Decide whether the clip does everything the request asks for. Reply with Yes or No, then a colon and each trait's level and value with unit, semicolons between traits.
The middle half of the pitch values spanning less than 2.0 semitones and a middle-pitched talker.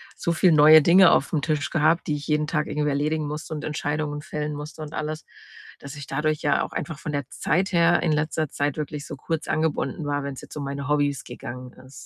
Yes: narrow, 1.5 semitones; medium, 150 Hz